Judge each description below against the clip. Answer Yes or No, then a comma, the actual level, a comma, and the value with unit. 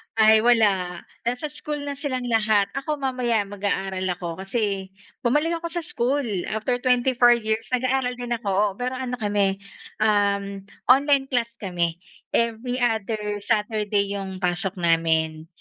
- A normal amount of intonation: Yes, average, 3.9 semitones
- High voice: Yes, high, 220 Hz